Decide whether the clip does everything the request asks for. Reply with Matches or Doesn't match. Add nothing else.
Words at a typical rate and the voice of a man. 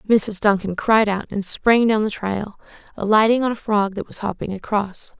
Doesn't match